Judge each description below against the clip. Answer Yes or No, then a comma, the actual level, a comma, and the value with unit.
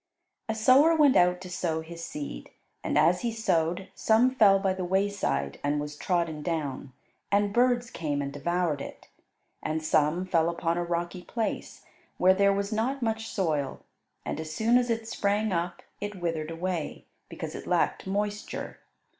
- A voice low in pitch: No, medium, 180 Hz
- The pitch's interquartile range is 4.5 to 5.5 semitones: Yes, average, 4.9 semitones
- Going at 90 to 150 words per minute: No, average, 170 wpm